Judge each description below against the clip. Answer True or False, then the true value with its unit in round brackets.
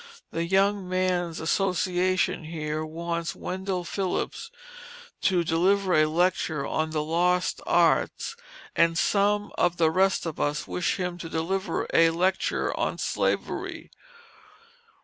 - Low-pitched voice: False (175 Hz)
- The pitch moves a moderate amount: False (2.3 semitones)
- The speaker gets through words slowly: True (125 wpm)